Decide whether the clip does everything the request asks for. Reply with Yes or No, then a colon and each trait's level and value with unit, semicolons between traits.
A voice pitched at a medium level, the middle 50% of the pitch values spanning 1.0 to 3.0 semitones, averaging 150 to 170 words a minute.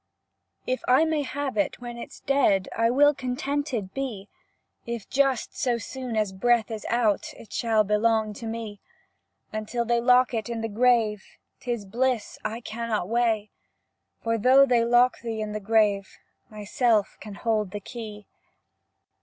No: high, 230 Hz; average, 2.7 semitones; average, 160 wpm